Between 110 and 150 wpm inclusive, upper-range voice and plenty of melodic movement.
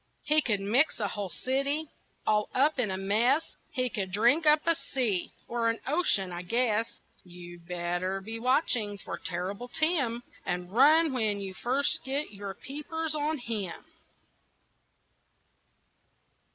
Yes: average, 140 wpm; high, 230 Hz; wide, 6.5 semitones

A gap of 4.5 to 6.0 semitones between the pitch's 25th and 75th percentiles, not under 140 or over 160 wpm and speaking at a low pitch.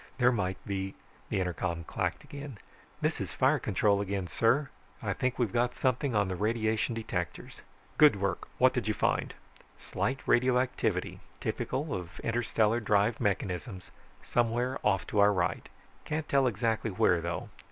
No: average, 4.1 semitones; average, 150 wpm; low, 110 Hz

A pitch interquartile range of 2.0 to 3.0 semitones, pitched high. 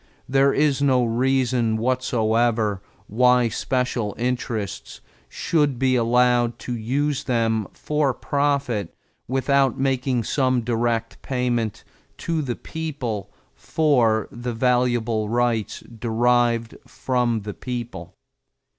No: narrow, 2.5 semitones; low, 120 Hz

